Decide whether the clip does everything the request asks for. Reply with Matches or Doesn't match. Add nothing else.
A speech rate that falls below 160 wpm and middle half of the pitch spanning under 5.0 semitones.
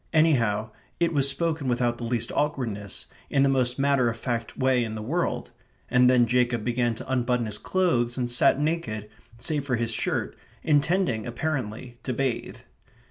Doesn't match